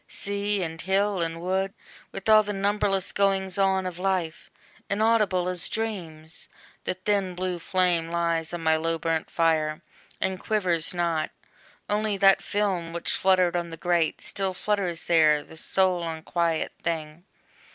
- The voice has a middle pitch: Yes, medium, 180 Hz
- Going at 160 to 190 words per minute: No, average, 150 wpm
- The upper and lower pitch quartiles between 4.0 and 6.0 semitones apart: No, average, 2.8 semitones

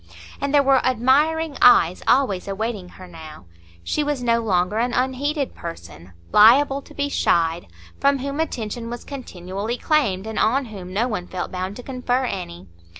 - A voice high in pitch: Yes, high, 235 Hz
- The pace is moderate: Yes, average, 165 wpm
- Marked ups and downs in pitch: Yes, wide, 6.7 semitones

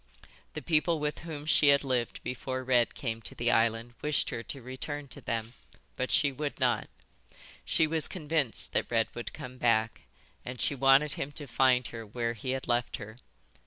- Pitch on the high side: No, low, 130 Hz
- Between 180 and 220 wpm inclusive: Yes, average, 190 wpm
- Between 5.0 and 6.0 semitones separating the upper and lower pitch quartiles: No, average, 3.7 semitones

